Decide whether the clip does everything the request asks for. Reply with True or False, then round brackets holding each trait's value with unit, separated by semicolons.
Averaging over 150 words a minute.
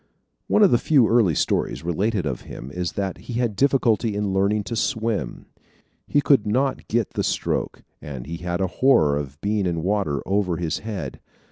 True (190 wpm)